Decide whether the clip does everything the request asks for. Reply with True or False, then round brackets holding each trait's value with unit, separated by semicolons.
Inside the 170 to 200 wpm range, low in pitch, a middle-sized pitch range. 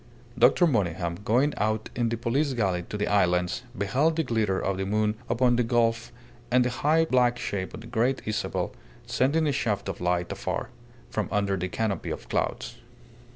True (185 wpm; 115 Hz; 4.2 semitones)